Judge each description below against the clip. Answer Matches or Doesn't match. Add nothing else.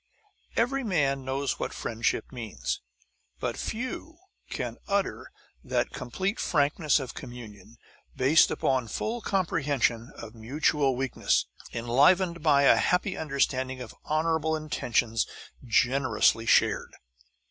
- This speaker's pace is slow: Matches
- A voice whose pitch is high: Doesn't match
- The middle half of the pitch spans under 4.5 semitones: Doesn't match